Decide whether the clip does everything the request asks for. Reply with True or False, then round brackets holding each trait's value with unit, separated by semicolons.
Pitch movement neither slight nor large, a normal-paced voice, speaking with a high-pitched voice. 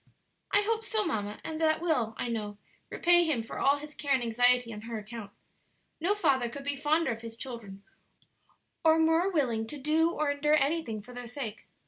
False (5.7 semitones; 195 wpm; 275 Hz)